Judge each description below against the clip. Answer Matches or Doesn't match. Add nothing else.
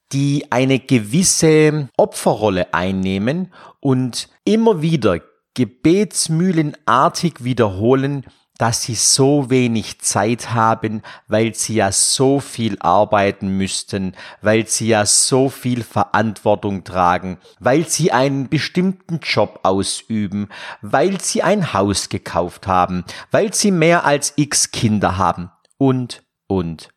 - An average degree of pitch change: Doesn't match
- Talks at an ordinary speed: Doesn't match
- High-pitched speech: Doesn't match